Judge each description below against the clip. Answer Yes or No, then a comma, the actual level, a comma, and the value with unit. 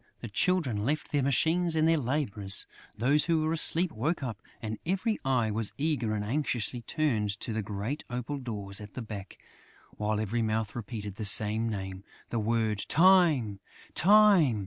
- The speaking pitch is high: No, low, 120 Hz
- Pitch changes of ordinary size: No, wide, 6.4 semitones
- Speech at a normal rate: Yes, average, 170 wpm